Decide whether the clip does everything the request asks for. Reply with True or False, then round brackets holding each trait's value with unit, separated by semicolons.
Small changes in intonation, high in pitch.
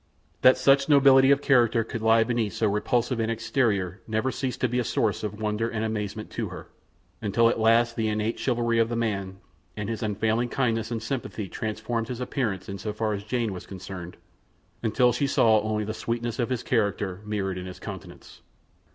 False (2.2 semitones; 110 Hz)